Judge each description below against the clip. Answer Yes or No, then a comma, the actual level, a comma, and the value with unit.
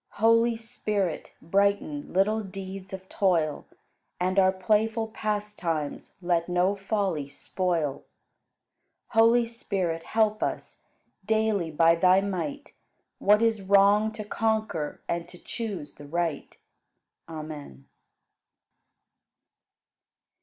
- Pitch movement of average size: Yes, average, 4.3 semitones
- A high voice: Yes, high, 195 Hz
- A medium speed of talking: No, slow, 100 wpm